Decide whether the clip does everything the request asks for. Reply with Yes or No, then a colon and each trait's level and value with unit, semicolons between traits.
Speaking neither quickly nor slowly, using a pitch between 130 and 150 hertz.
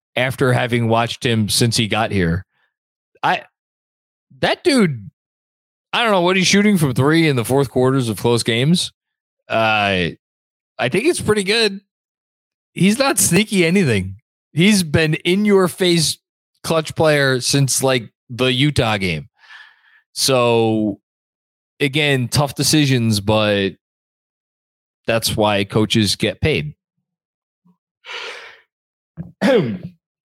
No: slow, 115 wpm; low, 135 Hz